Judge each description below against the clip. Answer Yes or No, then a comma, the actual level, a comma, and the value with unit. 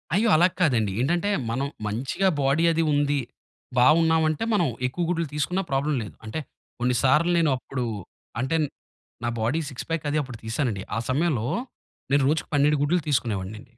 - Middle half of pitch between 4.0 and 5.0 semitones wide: Yes, average, 4.5 semitones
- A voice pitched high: No, medium, 145 Hz